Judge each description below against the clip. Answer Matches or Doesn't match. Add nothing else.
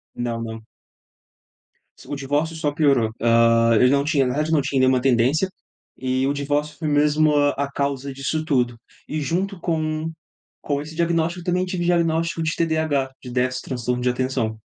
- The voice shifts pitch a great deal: Doesn't match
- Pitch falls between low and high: Matches